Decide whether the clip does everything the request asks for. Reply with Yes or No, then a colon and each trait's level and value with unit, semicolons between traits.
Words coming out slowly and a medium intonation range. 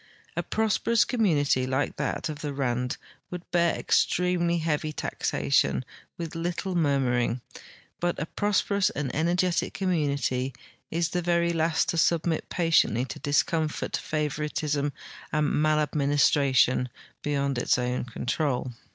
Yes: slow, 125 wpm; average, 3.9 semitones